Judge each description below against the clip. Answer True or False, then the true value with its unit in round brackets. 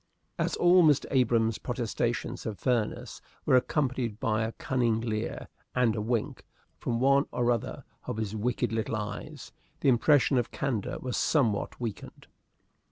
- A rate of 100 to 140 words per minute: False (150 wpm)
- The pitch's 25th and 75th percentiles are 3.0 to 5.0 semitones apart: False (2.5 semitones)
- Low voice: True (120 Hz)